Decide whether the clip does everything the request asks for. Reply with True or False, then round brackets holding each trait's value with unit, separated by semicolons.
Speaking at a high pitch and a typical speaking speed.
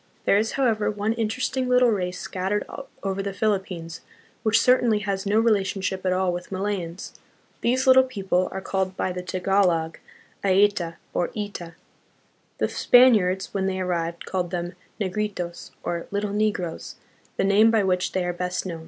True (195 Hz; 160 wpm)